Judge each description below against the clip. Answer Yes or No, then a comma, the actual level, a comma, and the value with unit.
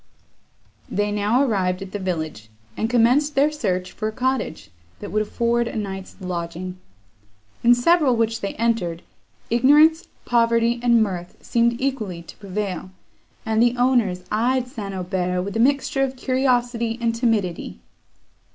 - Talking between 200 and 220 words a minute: No, average, 145 wpm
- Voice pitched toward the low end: No, high, 225 Hz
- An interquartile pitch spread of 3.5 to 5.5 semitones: Yes, average, 4.5 semitones